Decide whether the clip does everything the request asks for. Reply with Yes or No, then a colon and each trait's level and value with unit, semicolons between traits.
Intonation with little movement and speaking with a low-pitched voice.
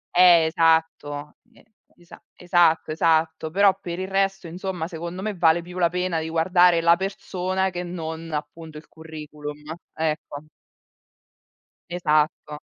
No: narrow, 2.2 semitones; medium, 165 Hz